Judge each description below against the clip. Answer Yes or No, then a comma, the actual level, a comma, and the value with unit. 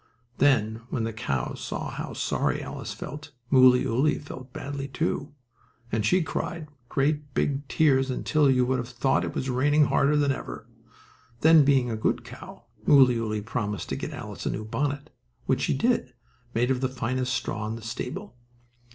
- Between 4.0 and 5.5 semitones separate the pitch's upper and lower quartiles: No, average, 3.5 semitones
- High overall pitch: No, low, 130 Hz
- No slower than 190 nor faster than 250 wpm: No, average, 170 wpm